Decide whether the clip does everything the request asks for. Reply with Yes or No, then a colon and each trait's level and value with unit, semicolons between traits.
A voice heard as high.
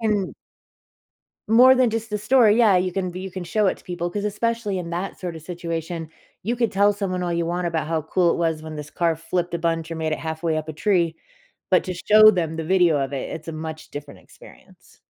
No: medium, 175 Hz